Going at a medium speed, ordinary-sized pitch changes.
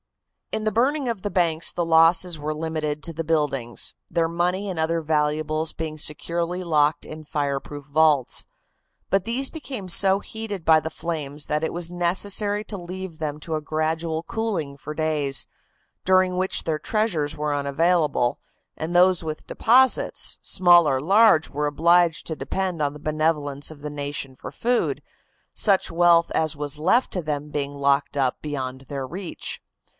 Yes: average, 165 wpm; average, 3.4 semitones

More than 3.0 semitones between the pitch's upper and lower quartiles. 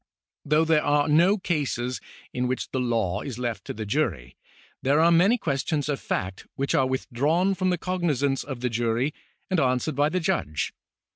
Yes: average, 4.7 semitones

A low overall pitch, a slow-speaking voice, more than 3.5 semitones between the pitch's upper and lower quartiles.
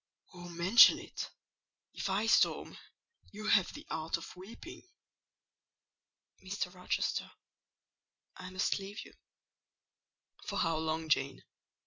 No: medium, 185 Hz; slow, 110 wpm; average, 3.9 semitones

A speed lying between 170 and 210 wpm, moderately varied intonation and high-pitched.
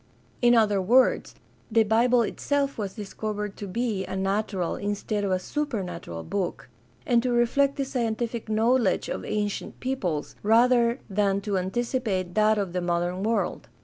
No: average, 150 wpm; average, 3.8 semitones; high, 215 Hz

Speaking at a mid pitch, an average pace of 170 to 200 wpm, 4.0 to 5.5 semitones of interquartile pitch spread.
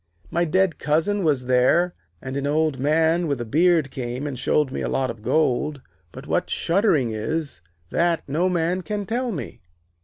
Yes: medium, 155 Hz; average, 180 wpm; average, 4.8 semitones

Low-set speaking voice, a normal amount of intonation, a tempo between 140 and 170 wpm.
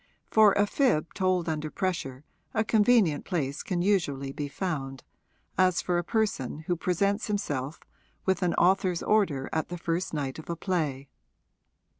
No: medium, 175 Hz; average, 4.9 semitones; average, 155 wpm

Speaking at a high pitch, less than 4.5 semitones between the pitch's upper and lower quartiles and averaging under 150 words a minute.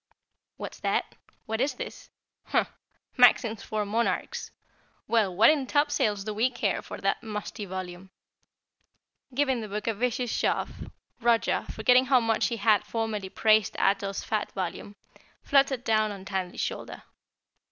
Yes: high, 220 Hz; average, 3.3 semitones; average, 140 wpm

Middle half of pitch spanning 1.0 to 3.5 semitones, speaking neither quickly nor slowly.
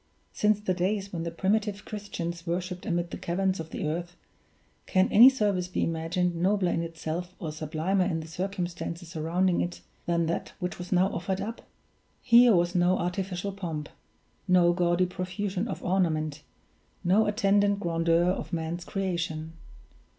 Yes: narrow, 2.4 semitones; average, 155 wpm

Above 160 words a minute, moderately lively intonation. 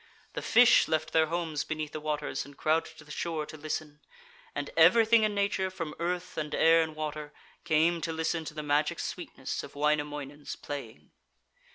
No: average, 180 wpm; narrow, 2.1 semitones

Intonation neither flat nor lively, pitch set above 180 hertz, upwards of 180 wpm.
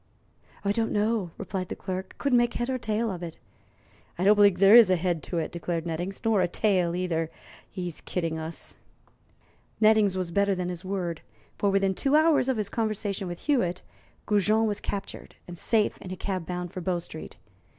Yes: average, 3.3 semitones; high, 190 Hz; average, 190 wpm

